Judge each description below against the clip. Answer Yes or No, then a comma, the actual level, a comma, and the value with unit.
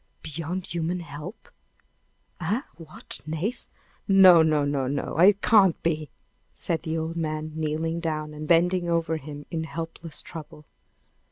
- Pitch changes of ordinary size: No, narrow, 2.0 semitones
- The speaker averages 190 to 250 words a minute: No, average, 140 wpm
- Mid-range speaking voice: Yes, medium, 160 Hz